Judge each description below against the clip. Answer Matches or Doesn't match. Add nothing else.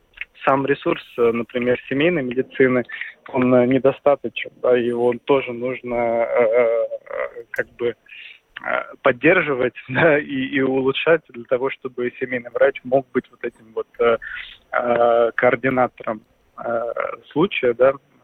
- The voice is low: Matches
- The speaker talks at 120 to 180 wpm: Doesn't match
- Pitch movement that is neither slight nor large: Matches